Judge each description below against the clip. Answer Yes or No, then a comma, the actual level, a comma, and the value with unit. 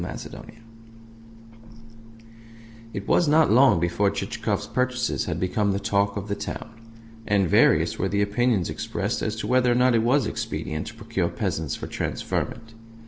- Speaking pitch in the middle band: No, low, 110 Hz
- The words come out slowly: No, average, 160 wpm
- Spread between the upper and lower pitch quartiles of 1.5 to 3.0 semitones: No, average, 3.6 semitones